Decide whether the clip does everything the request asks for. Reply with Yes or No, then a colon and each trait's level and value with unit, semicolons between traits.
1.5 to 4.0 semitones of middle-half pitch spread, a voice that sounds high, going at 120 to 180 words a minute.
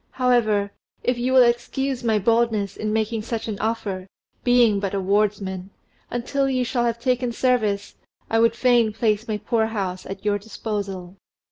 Yes: average, 2.9 semitones; high, 220 Hz; average, 165 wpm